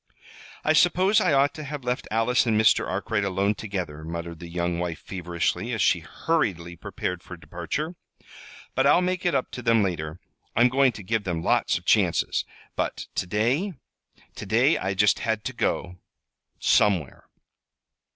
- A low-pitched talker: Yes, low, 105 Hz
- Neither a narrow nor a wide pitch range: No, wide, 6.9 semitones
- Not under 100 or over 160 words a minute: No, average, 170 wpm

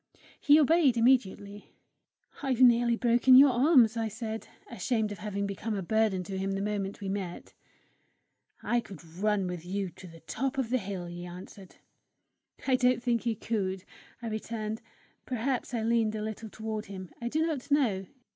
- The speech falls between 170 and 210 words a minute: Yes, average, 175 wpm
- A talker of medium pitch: No, high, 220 Hz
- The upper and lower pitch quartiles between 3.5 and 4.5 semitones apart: Yes, average, 3.8 semitones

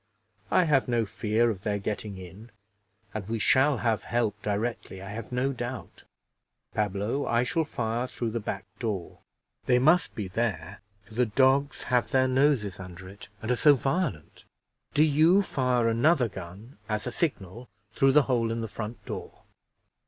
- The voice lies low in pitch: Yes, low, 115 Hz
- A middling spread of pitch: Yes, average, 3.9 semitones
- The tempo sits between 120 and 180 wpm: Yes, average, 170 wpm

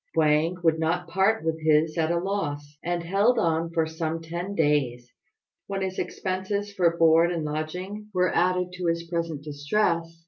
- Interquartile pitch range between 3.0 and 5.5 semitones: No, narrow, 2.5 semitones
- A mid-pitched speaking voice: Yes, medium, 170 Hz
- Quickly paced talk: No, average, 170 wpm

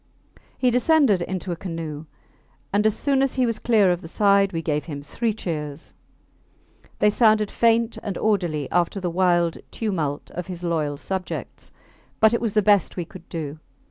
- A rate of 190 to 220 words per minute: No, average, 175 wpm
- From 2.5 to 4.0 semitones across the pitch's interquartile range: No, average, 4.7 semitones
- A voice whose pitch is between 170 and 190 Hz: Yes, medium, 185 Hz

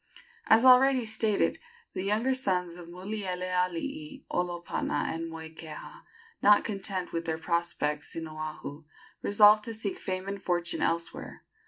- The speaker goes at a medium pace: No, slow, 130 wpm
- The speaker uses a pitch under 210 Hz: Yes, medium, 185 Hz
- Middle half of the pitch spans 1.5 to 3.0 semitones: No, average, 4.2 semitones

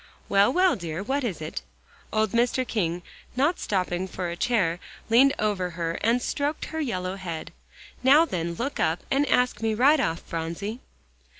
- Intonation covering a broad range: Yes, wide, 6.7 semitones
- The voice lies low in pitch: No, high, 210 Hz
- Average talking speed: Yes, average, 170 wpm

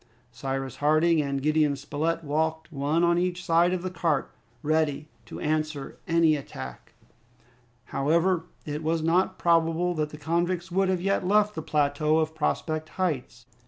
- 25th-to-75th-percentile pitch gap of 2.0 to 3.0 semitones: Yes, narrow, 2.5 semitones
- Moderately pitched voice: Yes, medium, 160 Hz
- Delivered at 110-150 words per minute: No, average, 160 wpm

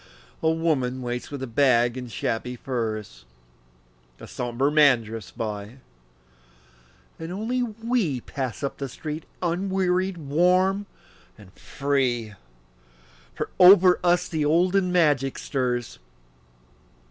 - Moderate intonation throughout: No, wide, 6.6 semitones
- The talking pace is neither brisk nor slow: No, slow, 110 wpm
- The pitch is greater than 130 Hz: Yes, medium, 140 Hz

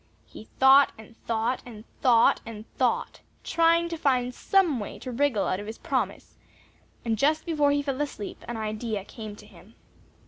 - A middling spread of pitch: Yes, average, 4.6 semitones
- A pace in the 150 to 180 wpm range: Yes, average, 175 wpm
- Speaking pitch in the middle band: No, high, 245 Hz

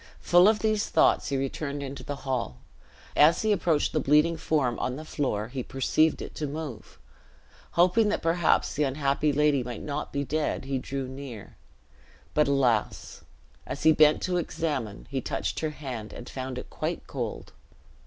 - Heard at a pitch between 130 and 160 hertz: Yes, medium, 140 Hz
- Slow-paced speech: No, average, 175 wpm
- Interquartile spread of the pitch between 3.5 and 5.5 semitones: No, average, 3.1 semitones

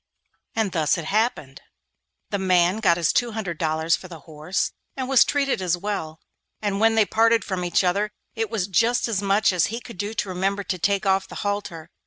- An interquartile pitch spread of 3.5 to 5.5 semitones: Yes, average, 4.1 semitones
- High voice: Yes, high, 195 Hz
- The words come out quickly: Yes, fast, 210 wpm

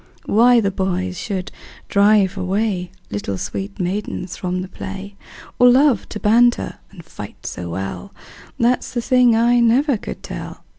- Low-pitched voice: No, high, 200 Hz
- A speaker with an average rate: Yes, average, 155 wpm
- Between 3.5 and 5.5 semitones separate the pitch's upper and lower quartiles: Yes, average, 4.6 semitones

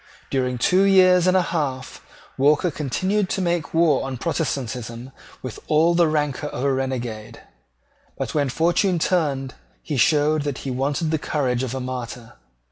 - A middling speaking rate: Yes, average, 160 wpm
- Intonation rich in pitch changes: No, average, 4.6 semitones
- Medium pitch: Yes, medium, 145 Hz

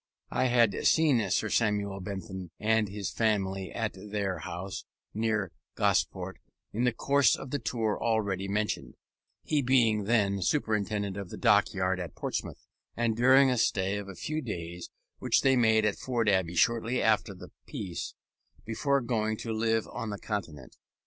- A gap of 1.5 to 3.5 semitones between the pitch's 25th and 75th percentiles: Yes, average, 3.1 semitones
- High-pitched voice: No, low, 105 Hz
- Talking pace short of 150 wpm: No, average, 160 wpm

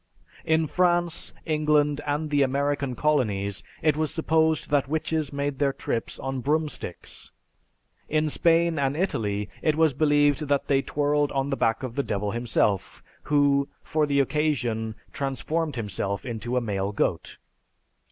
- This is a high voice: No, medium, 145 Hz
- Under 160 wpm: Yes, average, 140 wpm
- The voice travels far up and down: No, average, 3.7 semitones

